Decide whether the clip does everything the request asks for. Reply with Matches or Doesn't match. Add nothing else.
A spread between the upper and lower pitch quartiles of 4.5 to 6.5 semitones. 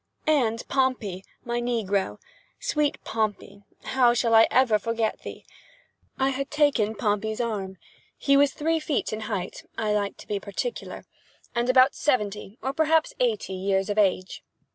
Matches